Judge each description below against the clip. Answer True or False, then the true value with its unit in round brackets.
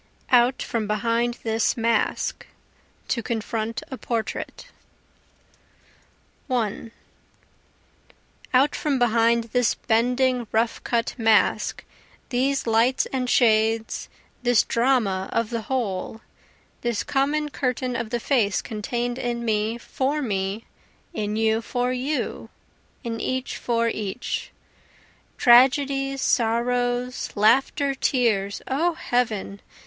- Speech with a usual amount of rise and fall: False (2.3 semitones)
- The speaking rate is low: True (105 wpm)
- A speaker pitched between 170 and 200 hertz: False (235 Hz)